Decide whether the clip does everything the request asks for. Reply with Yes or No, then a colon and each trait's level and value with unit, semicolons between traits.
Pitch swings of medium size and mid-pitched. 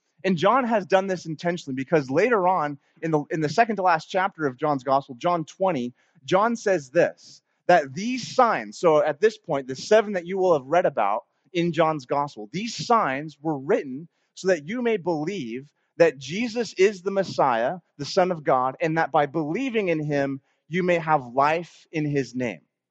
Yes: average, 4.8 semitones; medium, 165 Hz